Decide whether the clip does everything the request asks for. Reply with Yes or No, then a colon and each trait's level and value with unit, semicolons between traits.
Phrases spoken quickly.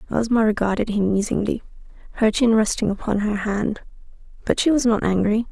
No: average, 165 wpm